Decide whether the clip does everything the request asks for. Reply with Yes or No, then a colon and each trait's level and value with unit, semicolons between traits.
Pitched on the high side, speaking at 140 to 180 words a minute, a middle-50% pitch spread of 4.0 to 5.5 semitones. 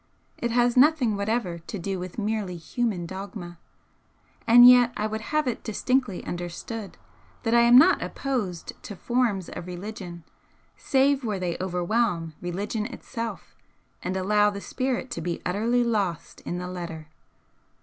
Yes: high, 210 Hz; average, 150 wpm; average, 5.1 semitones